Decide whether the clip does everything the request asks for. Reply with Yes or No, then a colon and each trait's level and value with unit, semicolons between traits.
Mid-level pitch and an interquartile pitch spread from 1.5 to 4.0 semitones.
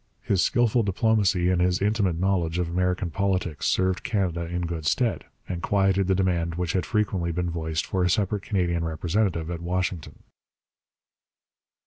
No: very low, 90 Hz; narrow, 2.4 semitones